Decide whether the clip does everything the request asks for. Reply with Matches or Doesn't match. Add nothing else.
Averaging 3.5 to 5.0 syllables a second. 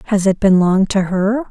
Matches